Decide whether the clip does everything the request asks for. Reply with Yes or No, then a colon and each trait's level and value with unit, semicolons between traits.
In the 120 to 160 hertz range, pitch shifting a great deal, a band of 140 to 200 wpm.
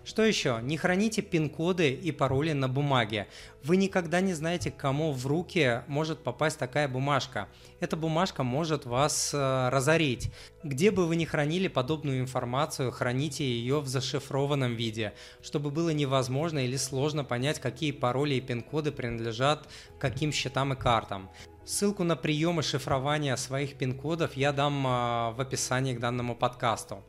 No: medium, 140 Hz; average, 3.7 semitones; average, 150 wpm